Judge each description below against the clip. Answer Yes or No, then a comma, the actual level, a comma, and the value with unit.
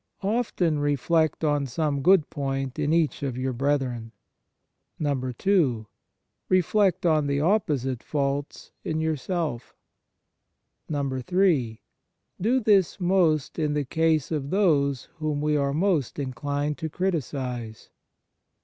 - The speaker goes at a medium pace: No, slow, 115 wpm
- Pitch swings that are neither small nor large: Yes, average, 3.6 semitones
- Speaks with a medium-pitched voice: Yes, medium, 150 Hz